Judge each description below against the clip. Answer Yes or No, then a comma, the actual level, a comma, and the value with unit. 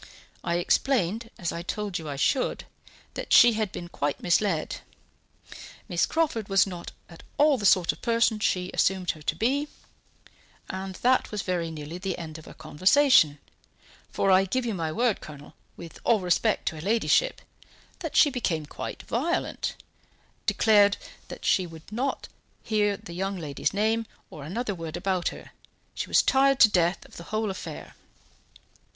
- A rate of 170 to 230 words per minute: Yes, average, 175 wpm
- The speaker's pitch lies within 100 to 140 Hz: No, high, 195 Hz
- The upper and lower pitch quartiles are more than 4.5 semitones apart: Yes, average, 5.0 semitones